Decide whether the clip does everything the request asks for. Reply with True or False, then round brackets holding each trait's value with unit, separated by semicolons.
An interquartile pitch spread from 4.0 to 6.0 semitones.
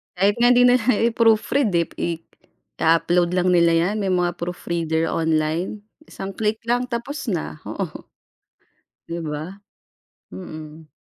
True (5.2 semitones)